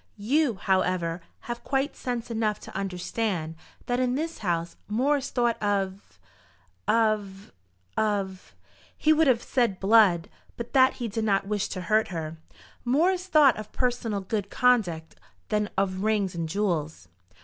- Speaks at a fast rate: No, average, 155 wpm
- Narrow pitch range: No, average, 4.4 semitones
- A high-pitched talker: Yes, high, 210 Hz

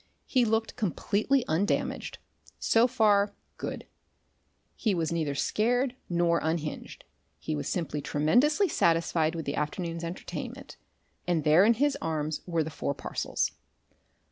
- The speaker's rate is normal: No, slow, 130 wpm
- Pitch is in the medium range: Yes, medium, 170 Hz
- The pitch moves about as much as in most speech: No, wide, 6.1 semitones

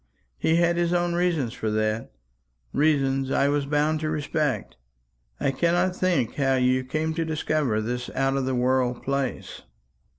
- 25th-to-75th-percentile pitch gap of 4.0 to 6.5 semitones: No, average, 3.6 semitones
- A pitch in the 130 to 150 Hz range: Yes, medium, 140 Hz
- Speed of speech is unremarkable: Yes, average, 160 wpm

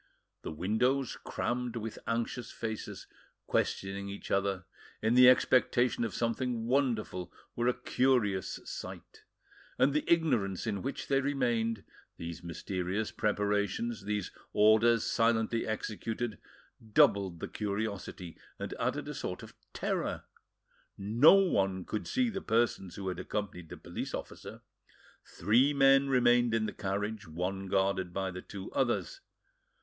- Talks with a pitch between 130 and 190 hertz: No, low, 110 Hz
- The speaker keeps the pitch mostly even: No, average, 3.9 semitones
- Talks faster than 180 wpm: No, slow, 135 wpm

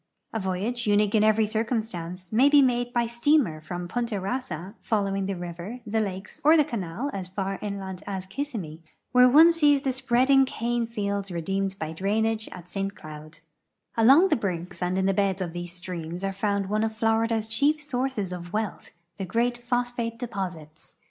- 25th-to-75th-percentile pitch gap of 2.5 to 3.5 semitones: No, average, 4.5 semitones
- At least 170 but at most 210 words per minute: Yes, average, 180 wpm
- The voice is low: No, high, 210 Hz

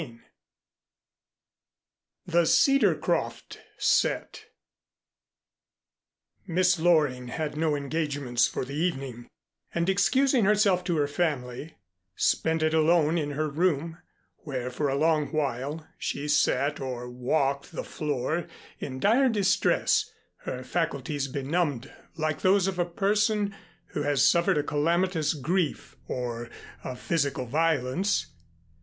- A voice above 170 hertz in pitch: No, medium, 155 Hz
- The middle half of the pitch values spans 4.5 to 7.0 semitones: No, average, 4.1 semitones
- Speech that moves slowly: Yes, slow, 115 wpm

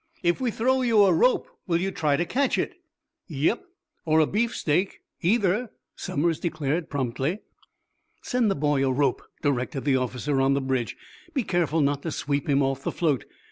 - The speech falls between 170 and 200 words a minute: Yes, average, 180 wpm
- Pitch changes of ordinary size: No, wide, 5.8 semitones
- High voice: No, medium, 155 Hz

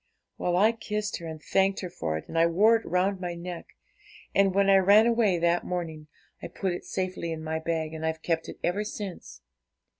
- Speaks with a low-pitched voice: No, medium, 180 Hz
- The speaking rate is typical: No, fast, 215 wpm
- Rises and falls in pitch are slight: No, average, 3.2 semitones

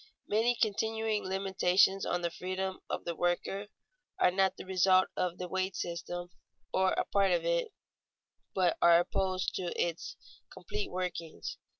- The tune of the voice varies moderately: No, narrow, 1.7 semitones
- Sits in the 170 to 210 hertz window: Yes, medium, 185 Hz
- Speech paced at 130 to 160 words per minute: Yes, average, 150 wpm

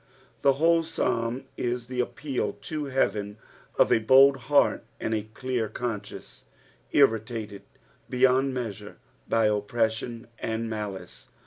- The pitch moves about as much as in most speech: Yes, average, 3.3 semitones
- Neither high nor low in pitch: No, low, 115 Hz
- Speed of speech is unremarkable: No, slow, 125 wpm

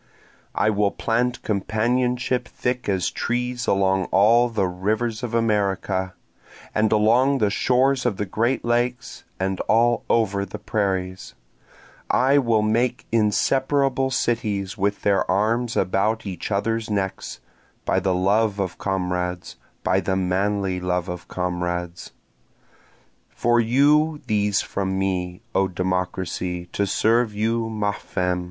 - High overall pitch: No, low, 105 Hz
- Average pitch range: Yes, average, 3.8 semitones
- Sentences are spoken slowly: Yes, slow, 130 wpm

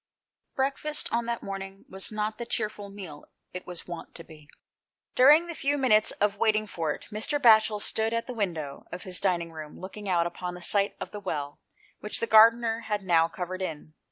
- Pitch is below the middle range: No, high, 200 Hz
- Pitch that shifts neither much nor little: Yes, average, 4.2 semitones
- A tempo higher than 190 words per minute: Yes, average, 200 wpm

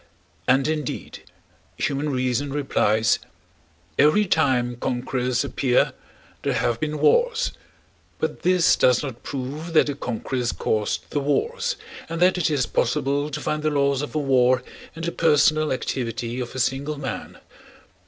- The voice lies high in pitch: No, medium, 140 Hz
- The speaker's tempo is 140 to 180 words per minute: Yes, average, 145 wpm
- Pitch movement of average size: Yes, average, 3.4 semitones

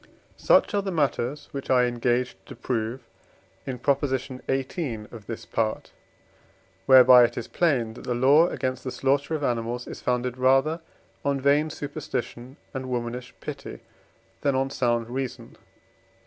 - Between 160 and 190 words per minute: No, average, 150 wpm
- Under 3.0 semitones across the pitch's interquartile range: Yes, narrow, 2.4 semitones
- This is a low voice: Yes, low, 130 Hz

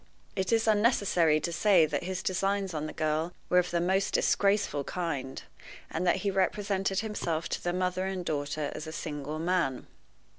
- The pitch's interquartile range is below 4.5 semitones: Yes, average, 3.7 semitones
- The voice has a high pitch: No, medium, 180 Hz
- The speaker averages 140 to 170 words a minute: No, average, 180 wpm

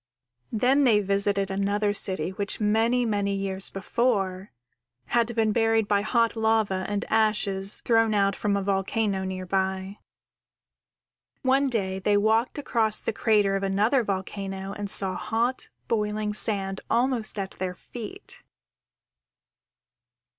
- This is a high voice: Yes, high, 205 Hz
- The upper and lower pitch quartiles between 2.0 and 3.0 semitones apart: Yes, narrow, 2.5 semitones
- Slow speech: Yes, slow, 130 wpm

